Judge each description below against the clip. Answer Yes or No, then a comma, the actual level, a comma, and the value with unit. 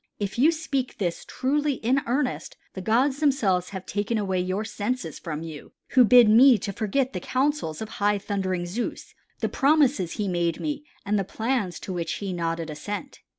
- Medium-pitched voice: No, high, 210 Hz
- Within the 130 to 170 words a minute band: No, average, 185 wpm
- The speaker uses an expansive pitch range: Yes, wide, 6.1 semitones